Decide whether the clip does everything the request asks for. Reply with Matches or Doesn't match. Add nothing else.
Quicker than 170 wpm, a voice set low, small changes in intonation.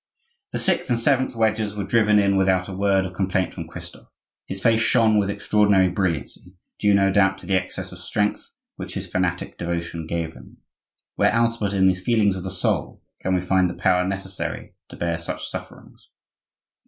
Matches